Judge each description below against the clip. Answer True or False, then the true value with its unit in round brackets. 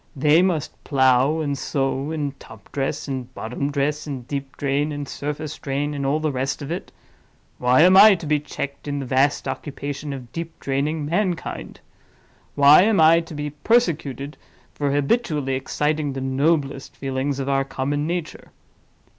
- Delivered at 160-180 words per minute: True (165 wpm)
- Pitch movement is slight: True (2.2 semitones)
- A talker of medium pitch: True (145 Hz)